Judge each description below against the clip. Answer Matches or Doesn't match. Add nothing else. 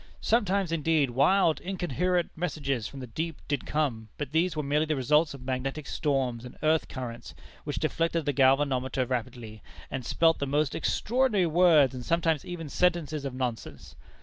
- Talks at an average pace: Matches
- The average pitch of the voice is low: Doesn't match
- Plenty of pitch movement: Doesn't match